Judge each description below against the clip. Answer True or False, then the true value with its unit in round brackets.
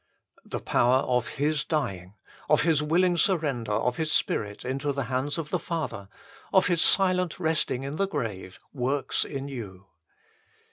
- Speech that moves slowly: False (155 wpm)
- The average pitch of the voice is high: False (140 Hz)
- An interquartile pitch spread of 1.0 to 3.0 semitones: False (4.7 semitones)